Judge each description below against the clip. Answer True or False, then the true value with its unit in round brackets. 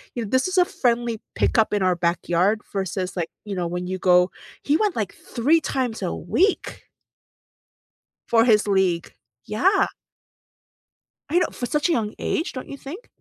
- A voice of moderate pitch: False (220 Hz)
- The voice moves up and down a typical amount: False (7.1 semitones)